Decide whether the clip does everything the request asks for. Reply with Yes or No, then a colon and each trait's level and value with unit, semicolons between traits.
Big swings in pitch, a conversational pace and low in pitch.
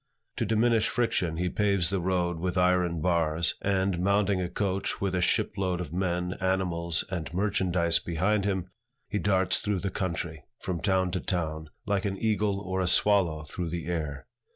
No: narrow, 2.4 semitones; average, 175 wpm; very low, 90 Hz